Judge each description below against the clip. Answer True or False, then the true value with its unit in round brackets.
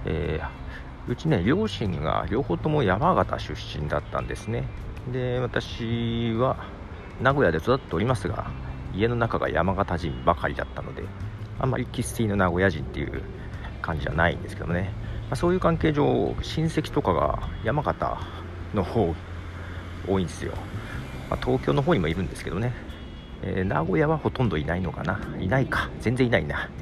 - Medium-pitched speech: False (95 Hz)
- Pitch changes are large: True (5.8 semitones)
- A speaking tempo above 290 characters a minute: True (330 characters per minute)